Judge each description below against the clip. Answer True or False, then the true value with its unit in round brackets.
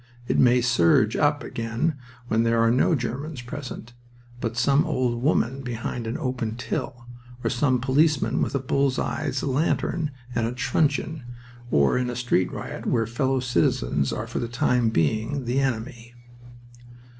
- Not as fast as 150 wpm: False (155 wpm)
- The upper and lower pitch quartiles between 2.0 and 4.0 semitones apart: True (3.0 semitones)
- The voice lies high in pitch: False (125 Hz)